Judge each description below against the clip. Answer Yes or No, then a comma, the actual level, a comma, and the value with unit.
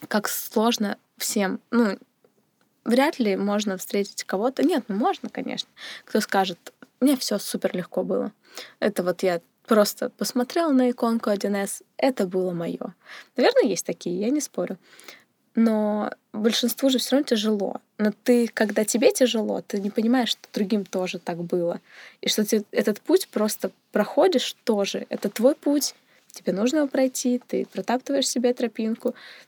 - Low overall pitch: No, high, 230 Hz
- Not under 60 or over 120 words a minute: No, average, 155 wpm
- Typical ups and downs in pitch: Yes, average, 3.6 semitones